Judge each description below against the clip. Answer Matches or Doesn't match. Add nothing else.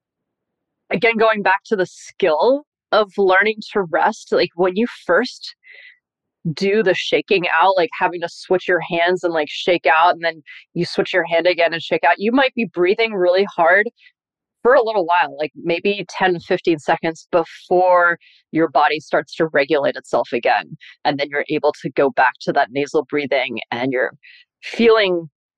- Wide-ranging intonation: Doesn't match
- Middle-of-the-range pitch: Matches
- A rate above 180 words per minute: Doesn't match